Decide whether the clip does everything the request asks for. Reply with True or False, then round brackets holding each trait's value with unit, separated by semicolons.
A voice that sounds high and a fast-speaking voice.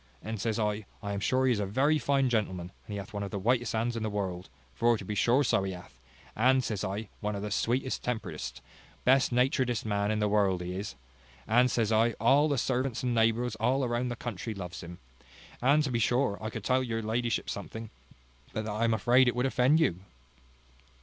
False (115 Hz; 225 wpm)